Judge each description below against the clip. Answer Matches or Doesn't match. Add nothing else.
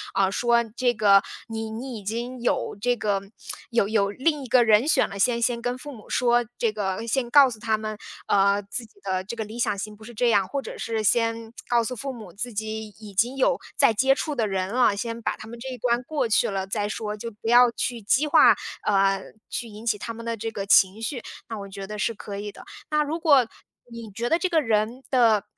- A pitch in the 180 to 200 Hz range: Doesn't match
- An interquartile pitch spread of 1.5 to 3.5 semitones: Matches